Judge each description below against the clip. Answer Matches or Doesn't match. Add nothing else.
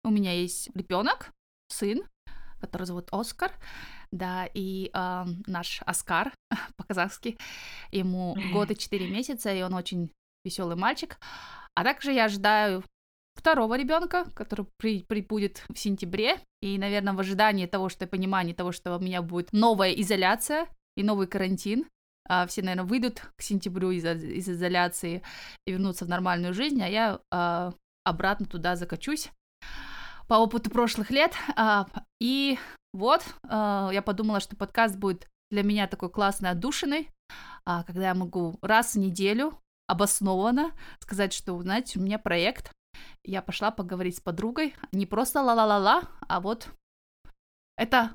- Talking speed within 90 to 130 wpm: Doesn't match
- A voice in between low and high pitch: Doesn't match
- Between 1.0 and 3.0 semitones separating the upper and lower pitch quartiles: Doesn't match